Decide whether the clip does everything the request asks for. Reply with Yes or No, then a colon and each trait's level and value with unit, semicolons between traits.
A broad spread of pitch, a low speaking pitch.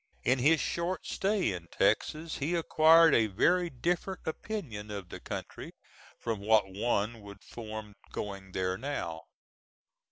Yes: wide, 8.3 semitones; low, 115 Hz